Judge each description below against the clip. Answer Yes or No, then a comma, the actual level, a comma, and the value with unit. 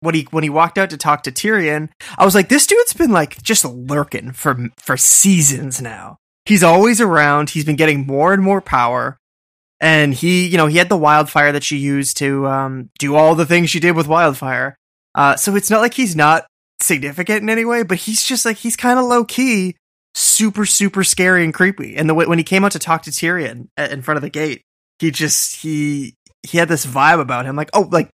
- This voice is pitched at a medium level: Yes, medium, 165 Hz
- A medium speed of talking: No, fast, 230 wpm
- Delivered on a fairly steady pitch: No, average, 5.3 semitones